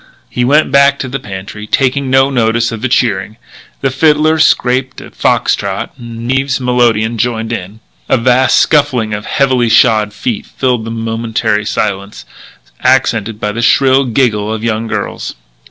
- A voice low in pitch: Yes, low, 120 Hz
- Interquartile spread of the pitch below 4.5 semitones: Yes, average, 3.1 semitones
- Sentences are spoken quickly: No, average, 160 wpm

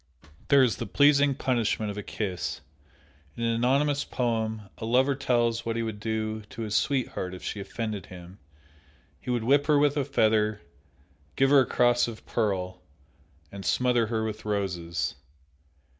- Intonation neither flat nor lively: Yes, average, 3.5 semitones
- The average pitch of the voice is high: No, low, 115 Hz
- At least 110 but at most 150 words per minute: No, average, 165 wpm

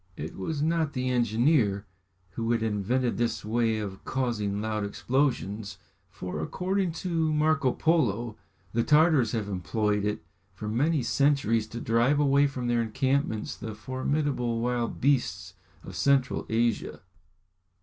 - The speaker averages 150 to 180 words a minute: No, slow, 135 wpm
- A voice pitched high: No, low, 120 Hz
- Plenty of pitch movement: No, average, 4.6 semitones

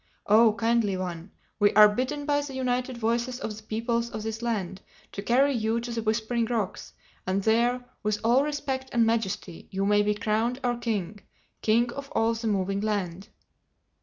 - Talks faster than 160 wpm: Yes, average, 175 wpm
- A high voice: Yes, high, 225 Hz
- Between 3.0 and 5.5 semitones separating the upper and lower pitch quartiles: No, narrow, 2.6 semitones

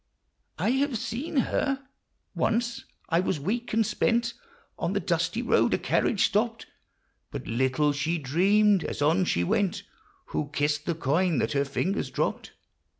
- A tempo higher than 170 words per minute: No, average, 150 wpm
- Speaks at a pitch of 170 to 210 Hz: Yes, medium, 185 Hz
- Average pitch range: No, wide, 7.8 semitones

